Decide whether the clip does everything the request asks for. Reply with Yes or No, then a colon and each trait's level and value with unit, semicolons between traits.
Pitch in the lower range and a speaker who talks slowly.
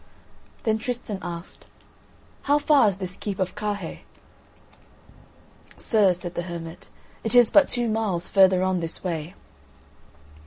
No: high, 190 Hz; slow, 130 wpm